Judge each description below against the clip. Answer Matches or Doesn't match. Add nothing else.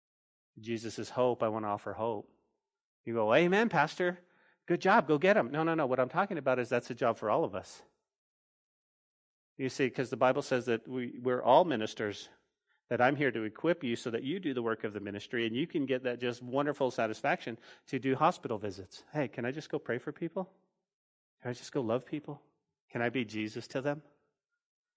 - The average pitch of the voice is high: Doesn't match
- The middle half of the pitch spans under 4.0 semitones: Doesn't match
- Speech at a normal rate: Doesn't match